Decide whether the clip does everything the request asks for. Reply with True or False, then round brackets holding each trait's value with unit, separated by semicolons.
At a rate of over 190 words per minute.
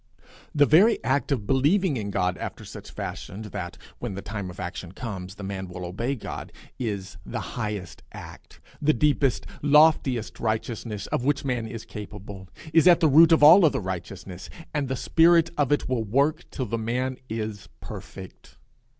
False (175 wpm)